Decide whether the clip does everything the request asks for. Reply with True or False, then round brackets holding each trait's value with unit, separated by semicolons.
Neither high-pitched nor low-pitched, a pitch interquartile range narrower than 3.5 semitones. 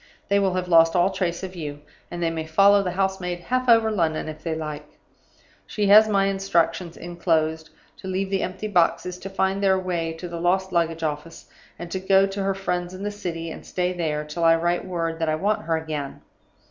True (175 Hz; 2.8 semitones)